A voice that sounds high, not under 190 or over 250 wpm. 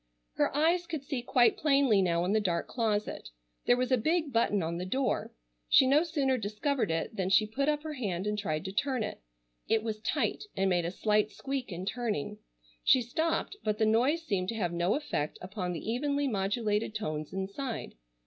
Yes: high, 220 Hz; average, 200 wpm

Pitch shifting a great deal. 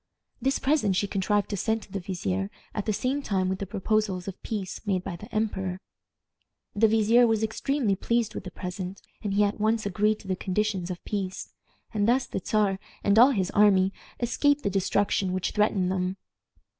No: average, 2.7 semitones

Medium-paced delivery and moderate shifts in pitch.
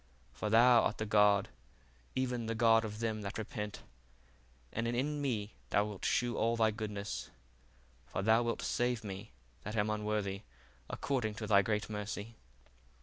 No: average, 155 wpm; narrow, 2.0 semitones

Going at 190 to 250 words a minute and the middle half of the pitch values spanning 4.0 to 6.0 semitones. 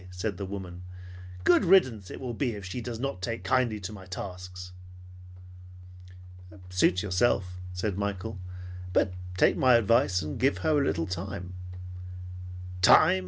No: average, 145 wpm; average, 4.6 semitones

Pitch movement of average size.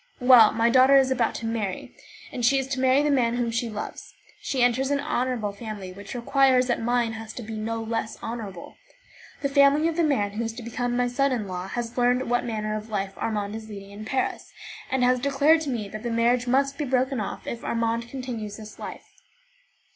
Yes: average, 3.0 semitones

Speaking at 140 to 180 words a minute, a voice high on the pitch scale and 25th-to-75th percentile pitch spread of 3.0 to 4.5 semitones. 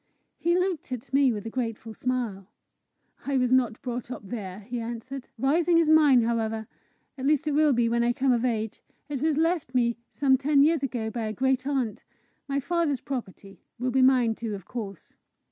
No: average, 195 wpm; very high, 250 Hz; average, 3.6 semitones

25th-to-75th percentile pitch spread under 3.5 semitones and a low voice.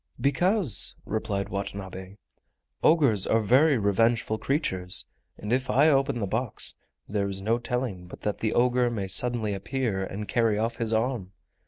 No: average, 4.2 semitones; low, 110 Hz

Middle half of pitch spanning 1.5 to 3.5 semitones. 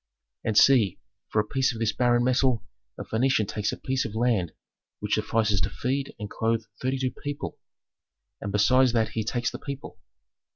Yes: average, 3.2 semitones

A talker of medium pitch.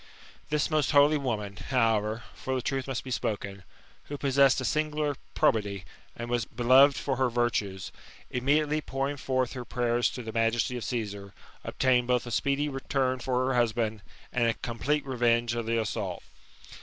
No: low, 125 Hz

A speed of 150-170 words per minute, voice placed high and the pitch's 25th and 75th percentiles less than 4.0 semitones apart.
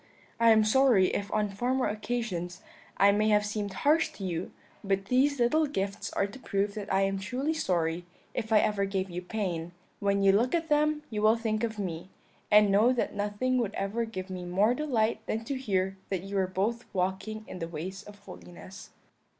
No: average, 200 wpm; high, 205 Hz; average, 3.4 semitones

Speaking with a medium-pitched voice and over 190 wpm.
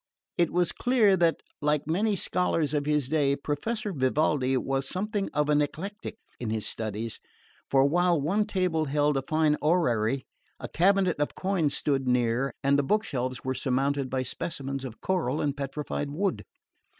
No: medium, 150 Hz; average, 165 wpm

